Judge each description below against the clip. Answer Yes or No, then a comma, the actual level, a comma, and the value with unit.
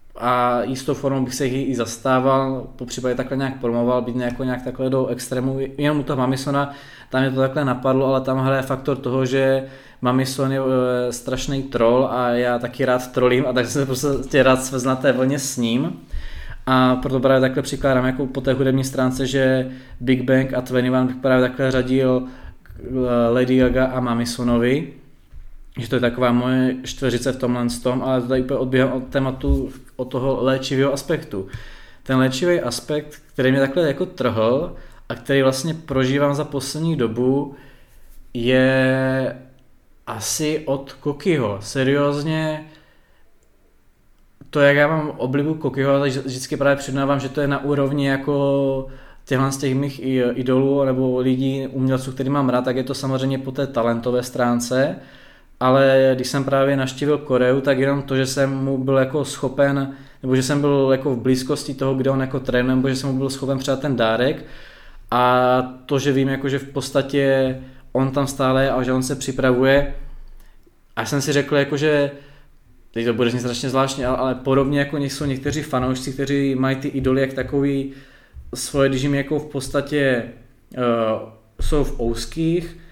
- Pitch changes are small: Yes, narrow, 1.5 semitones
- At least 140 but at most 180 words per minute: Yes, fast, 170 wpm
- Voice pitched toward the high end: No, low, 130 Hz